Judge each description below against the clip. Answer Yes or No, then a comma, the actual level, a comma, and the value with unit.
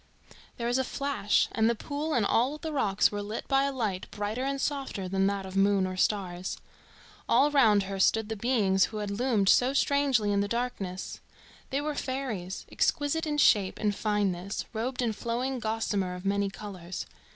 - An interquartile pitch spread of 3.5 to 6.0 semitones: Yes, average, 5.0 semitones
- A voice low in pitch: No, high, 215 Hz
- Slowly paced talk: No, average, 185 wpm